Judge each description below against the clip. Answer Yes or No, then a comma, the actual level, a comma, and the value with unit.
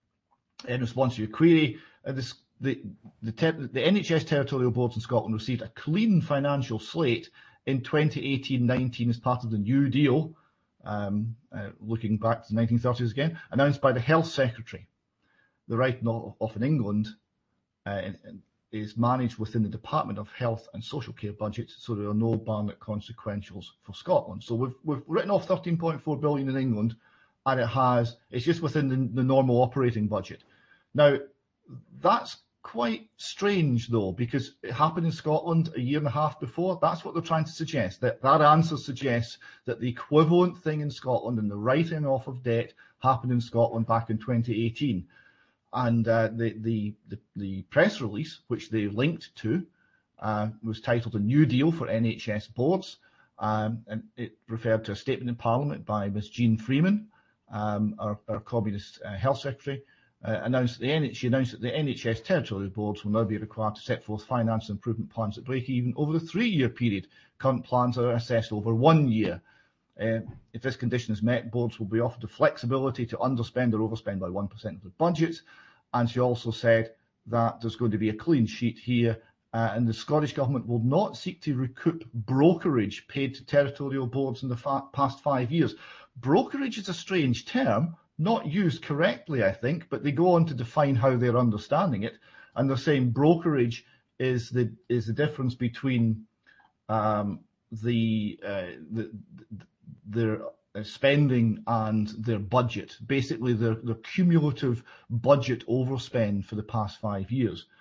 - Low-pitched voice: Yes, low, 120 Hz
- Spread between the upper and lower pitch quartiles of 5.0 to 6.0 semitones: No, average, 4.0 semitones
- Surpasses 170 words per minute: Yes, average, 180 wpm